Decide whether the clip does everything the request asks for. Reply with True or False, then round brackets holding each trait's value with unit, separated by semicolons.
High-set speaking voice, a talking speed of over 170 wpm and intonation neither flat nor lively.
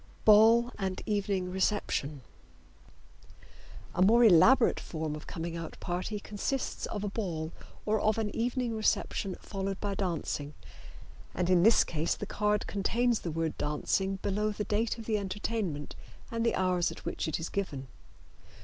False (200 Hz; 155 wpm; 3.9 semitones)